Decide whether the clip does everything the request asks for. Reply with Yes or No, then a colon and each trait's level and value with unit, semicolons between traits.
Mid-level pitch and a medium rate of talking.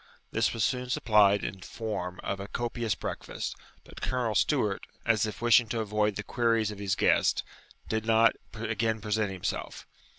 No: low, 110 Hz; average, 165 wpm